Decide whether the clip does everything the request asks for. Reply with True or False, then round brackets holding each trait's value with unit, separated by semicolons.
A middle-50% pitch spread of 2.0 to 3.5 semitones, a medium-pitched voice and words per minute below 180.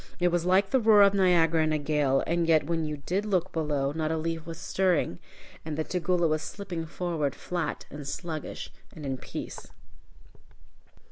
False (2.8 semitones; 165 Hz; 185 wpm)